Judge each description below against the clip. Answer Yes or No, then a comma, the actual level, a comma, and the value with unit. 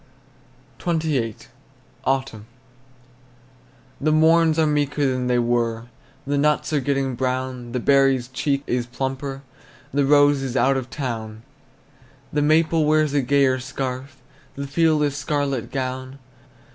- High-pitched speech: No, low, 135 Hz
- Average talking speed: No, slow, 130 wpm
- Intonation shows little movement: Yes, narrow, 2.3 semitones